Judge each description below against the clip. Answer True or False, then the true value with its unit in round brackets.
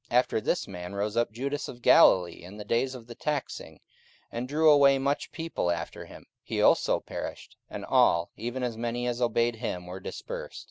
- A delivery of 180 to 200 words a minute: True (195 wpm)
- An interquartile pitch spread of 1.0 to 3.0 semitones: False (4.7 semitones)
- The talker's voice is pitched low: True (120 Hz)